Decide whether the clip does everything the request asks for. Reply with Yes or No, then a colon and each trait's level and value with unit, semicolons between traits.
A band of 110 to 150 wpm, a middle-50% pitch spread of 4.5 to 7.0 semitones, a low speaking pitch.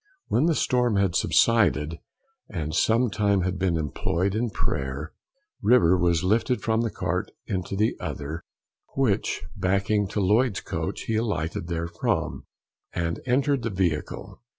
Yes: average, 140 wpm; average, 5.1 semitones; low, 100 Hz